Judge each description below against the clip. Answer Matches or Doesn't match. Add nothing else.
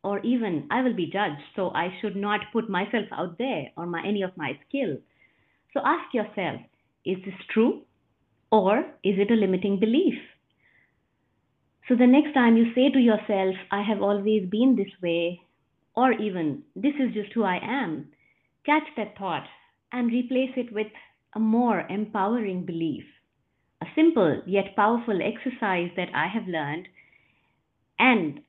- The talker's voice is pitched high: Matches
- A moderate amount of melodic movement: Matches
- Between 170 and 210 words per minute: Doesn't match